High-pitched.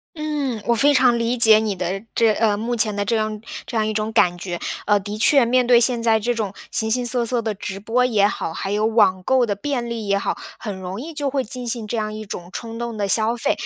Yes: high, 220 Hz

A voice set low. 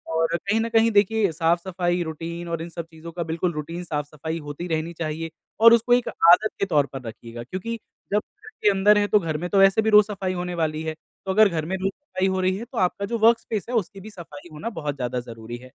No: medium, 175 Hz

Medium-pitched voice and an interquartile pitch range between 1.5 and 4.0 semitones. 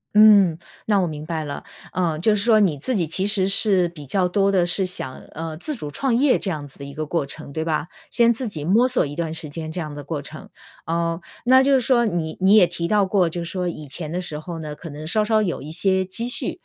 No: medium, 175 Hz; average, 4.7 semitones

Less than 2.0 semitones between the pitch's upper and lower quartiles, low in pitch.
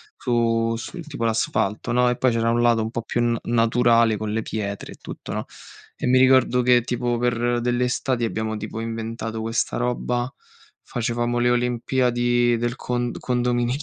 Yes: narrow, 1.2 semitones; low, 120 Hz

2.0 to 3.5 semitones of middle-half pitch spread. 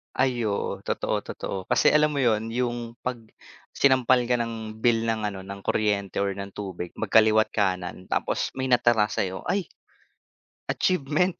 No: average, 4.0 semitones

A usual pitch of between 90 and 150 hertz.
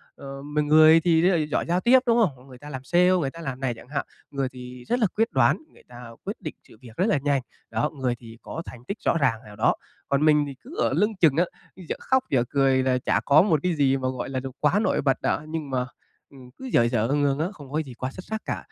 Yes: medium, 140 Hz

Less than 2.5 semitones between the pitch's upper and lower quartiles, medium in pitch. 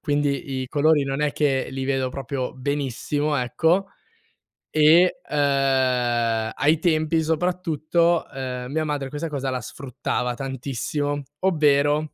No: average, 2.8 semitones; medium, 145 Hz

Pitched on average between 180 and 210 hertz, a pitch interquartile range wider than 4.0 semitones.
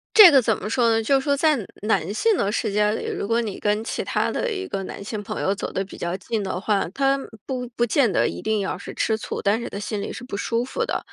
No: high, 220 Hz; average, 4.6 semitones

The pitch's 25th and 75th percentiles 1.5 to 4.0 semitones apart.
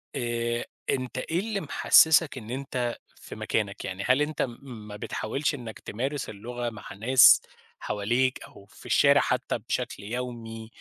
Yes: average, 3.0 semitones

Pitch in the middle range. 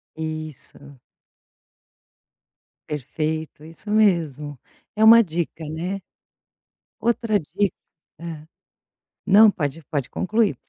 Yes: medium, 160 Hz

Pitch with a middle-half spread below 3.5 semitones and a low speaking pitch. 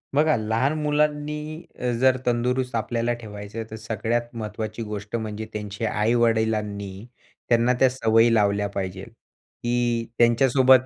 Yes: average, 2.8 semitones; low, 115 Hz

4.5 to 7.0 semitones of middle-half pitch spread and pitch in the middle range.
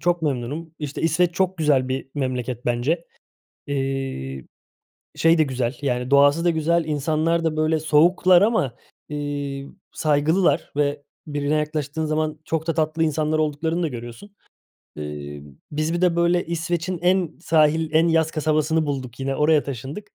No: average, 2.9 semitones; medium, 155 Hz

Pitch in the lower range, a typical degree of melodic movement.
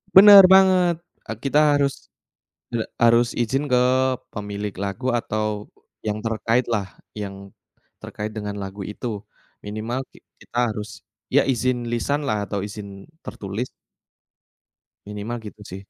Yes: low, 110 Hz; average, 3.4 semitones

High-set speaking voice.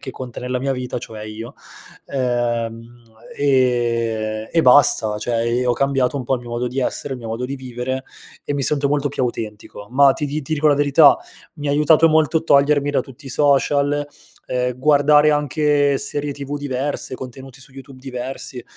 No: low, 135 Hz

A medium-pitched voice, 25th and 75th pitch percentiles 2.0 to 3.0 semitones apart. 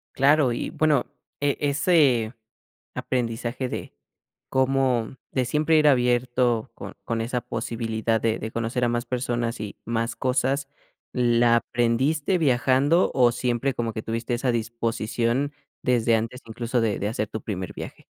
No: low, 120 Hz; narrow, 2.4 semitones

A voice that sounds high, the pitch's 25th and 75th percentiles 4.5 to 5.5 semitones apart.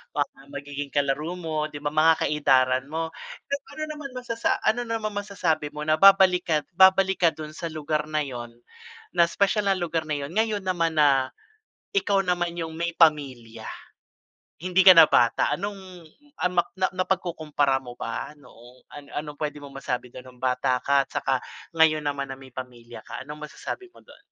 No: medium, 155 Hz; average, 4.9 semitones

